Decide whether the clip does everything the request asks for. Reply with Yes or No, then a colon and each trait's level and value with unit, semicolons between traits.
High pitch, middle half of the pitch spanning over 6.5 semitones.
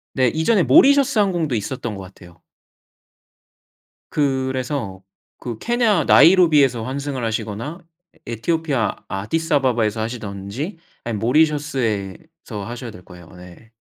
No: low, 130 Hz; wide, 6.9 semitones